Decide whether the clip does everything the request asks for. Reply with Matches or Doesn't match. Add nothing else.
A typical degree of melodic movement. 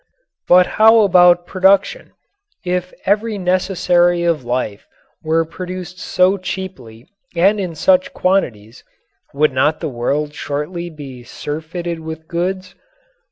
Matches